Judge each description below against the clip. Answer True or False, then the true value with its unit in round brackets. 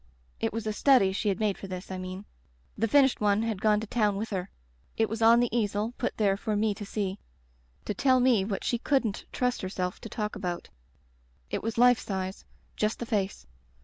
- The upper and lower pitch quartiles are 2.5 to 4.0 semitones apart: True (2.8 semitones)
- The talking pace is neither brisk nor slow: False (220 wpm)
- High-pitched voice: True (210 Hz)